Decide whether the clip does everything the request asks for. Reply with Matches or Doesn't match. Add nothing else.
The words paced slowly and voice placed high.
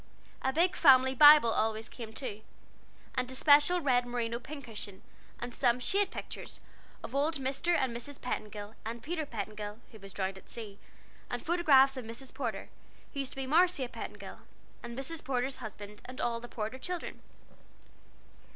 Doesn't match